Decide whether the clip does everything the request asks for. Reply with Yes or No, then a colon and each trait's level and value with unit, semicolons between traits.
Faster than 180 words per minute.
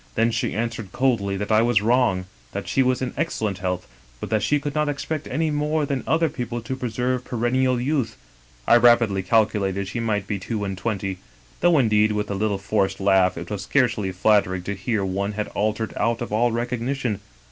Yes: average, 200 wpm